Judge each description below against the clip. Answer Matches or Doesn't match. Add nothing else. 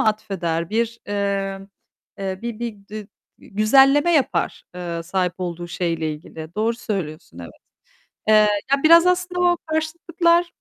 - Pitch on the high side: Matches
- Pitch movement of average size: Doesn't match